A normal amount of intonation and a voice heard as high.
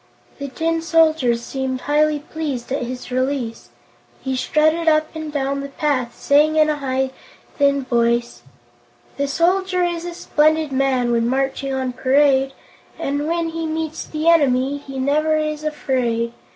Yes: average, 3.1 semitones; very high, 280 Hz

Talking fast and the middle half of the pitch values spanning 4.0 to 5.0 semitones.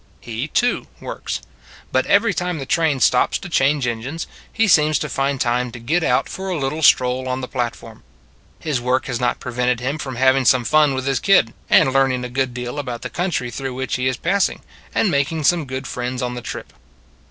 No: fast, 215 wpm; average, 3.6 semitones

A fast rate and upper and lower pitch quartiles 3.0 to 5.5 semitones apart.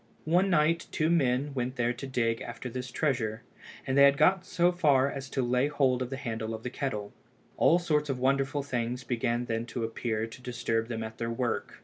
Yes: fast, 215 wpm; average, 3.3 semitones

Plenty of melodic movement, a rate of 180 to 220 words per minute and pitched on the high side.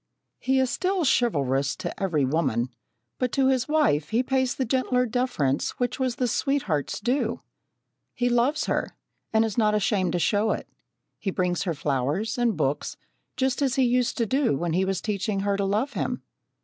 Yes: wide, 6.3 semitones; average, 185 wpm; high, 225 Hz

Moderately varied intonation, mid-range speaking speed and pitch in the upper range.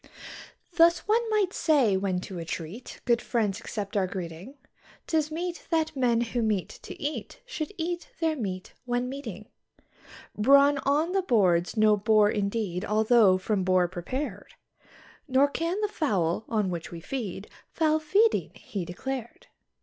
No: wide, 7.8 semitones; average, 150 wpm; high, 230 Hz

